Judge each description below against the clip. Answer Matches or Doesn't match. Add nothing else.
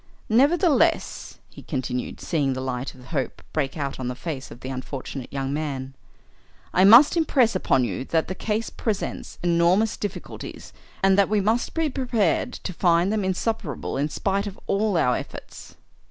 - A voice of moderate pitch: Matches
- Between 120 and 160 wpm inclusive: Doesn't match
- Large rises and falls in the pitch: Matches